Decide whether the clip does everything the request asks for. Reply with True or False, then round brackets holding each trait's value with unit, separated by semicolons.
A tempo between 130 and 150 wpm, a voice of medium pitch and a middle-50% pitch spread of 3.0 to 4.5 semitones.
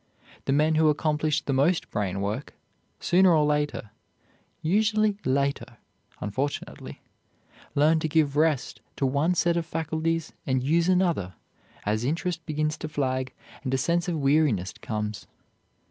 True (140 wpm; 150 Hz; 3.8 semitones)